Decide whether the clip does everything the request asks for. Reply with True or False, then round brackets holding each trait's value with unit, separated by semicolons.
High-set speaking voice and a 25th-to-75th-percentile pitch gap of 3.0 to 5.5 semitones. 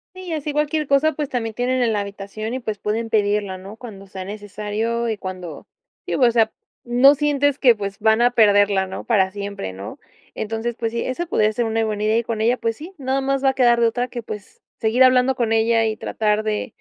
True (225 Hz; 3.4 semitones)